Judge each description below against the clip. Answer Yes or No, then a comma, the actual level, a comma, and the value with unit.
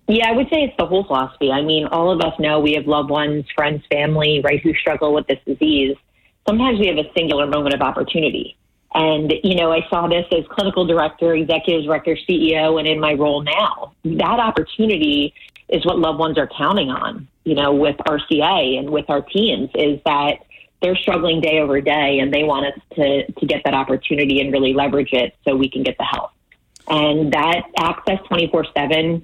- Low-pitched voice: No, medium, 155 Hz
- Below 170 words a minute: No, average, 200 wpm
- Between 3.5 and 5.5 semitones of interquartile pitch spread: No, average, 2.7 semitones